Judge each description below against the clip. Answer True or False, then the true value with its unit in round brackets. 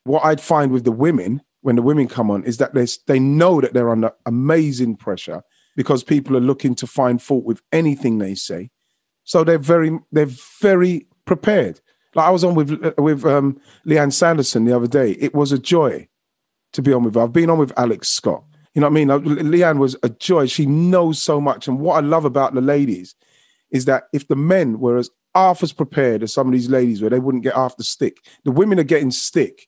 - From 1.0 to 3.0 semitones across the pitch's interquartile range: False (4.1 semitones)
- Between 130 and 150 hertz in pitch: True (140 Hz)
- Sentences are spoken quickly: True (225 wpm)